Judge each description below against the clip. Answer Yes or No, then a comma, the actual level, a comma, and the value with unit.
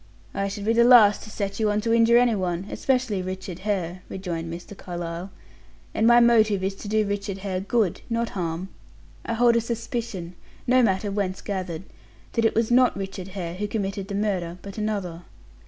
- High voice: Yes, high, 200 Hz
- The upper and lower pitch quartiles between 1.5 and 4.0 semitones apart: Yes, average, 3.5 semitones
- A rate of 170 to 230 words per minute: Yes, average, 190 wpm